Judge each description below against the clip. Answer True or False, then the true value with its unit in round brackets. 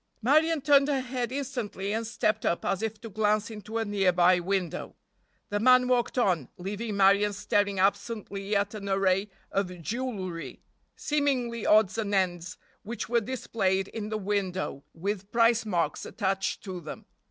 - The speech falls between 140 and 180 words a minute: True (155 wpm)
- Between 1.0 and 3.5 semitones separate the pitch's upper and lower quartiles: True (3.2 semitones)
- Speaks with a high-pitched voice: True (205 Hz)